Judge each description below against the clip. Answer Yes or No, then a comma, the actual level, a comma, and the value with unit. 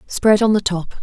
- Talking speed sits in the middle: No, fast, 235 wpm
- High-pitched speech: Yes, high, 200 Hz